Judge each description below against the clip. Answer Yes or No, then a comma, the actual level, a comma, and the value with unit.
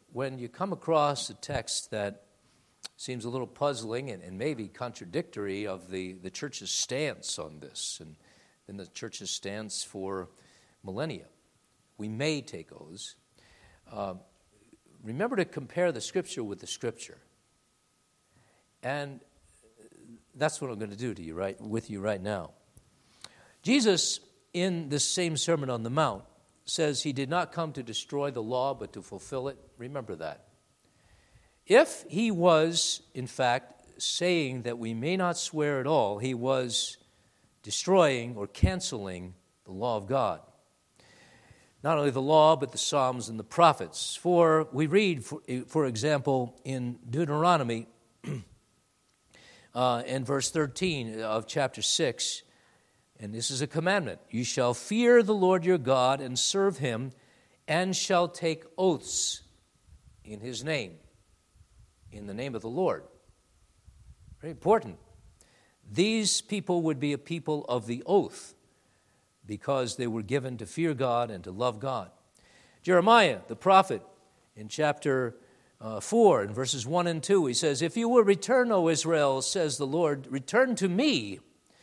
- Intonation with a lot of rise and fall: Yes, wide, 6.4 semitones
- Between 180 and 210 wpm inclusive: No, average, 145 wpm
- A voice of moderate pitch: No, low, 130 Hz